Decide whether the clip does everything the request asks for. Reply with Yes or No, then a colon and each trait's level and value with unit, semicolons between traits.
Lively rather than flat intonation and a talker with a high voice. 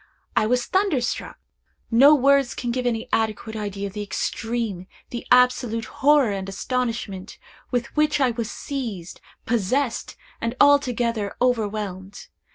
No: average, 3.3 semitones; high, 235 Hz